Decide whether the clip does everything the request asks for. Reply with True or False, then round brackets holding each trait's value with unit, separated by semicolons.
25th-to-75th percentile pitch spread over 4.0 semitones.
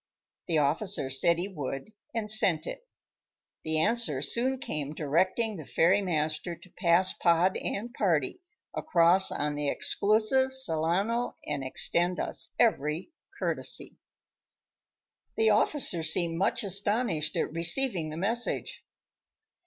True (5.6 semitones)